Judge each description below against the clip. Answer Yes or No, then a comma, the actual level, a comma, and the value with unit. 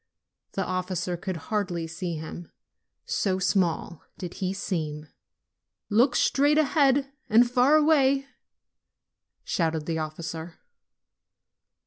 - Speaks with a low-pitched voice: No, medium, 185 Hz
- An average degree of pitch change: No, wide, 7.2 semitones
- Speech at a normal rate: No, slow, 100 wpm